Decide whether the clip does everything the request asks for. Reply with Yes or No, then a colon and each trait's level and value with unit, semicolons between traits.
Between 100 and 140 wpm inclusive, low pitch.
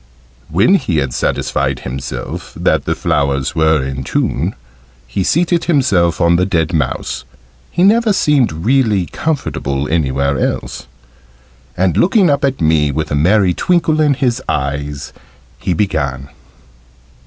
Yes: slow, 135 wpm; very low, 85 Hz